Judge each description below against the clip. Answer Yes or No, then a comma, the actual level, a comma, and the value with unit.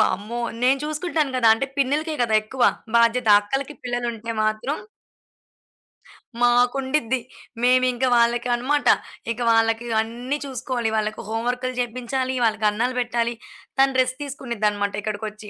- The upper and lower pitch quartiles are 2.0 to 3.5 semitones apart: Yes, narrow, 2.6 semitones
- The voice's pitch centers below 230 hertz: No, high, 245 Hz